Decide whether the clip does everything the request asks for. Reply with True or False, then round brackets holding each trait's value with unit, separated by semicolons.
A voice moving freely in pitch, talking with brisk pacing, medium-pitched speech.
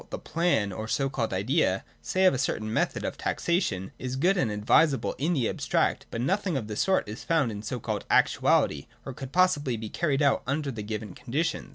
False (6.9 semitones; 220 wpm; 130 Hz)